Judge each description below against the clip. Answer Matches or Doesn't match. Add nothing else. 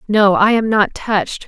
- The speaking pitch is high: Matches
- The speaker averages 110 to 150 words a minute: Doesn't match